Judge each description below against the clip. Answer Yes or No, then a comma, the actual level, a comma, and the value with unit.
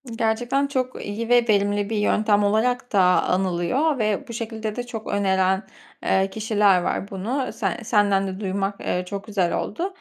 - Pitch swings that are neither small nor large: Yes, average, 3.1 semitones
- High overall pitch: Yes, high, 210 Hz